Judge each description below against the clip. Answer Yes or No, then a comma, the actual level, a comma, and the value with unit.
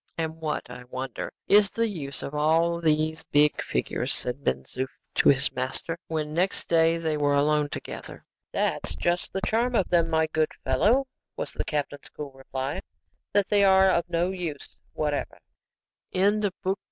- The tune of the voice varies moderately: Yes, average, 4.4 semitones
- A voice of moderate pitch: Yes, medium, 160 Hz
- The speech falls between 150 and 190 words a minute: Yes, average, 170 wpm